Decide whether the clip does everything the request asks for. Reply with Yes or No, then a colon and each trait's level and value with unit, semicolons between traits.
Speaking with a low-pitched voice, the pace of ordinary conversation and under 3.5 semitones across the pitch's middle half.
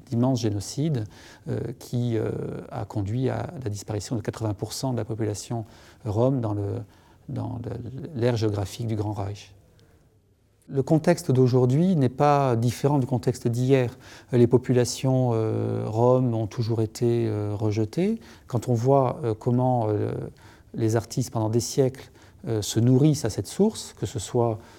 Yes: low, 120 Hz; average, 155 wpm; average, 2.8 semitones